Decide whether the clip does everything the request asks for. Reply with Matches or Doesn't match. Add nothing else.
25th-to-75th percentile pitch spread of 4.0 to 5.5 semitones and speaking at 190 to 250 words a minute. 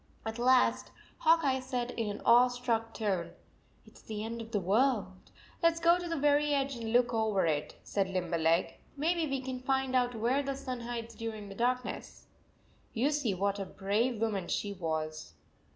Matches